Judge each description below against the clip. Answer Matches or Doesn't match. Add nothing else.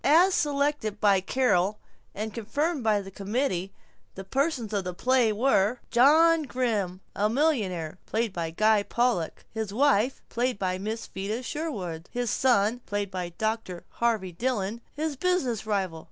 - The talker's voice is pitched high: Matches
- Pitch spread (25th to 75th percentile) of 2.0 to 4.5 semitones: Doesn't match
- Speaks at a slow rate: Matches